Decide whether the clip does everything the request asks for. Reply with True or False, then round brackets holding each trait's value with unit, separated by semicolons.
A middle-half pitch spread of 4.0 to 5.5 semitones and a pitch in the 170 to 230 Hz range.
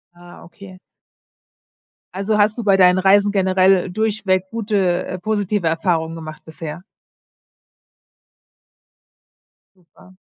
False (2.6 semitones; 185 Hz)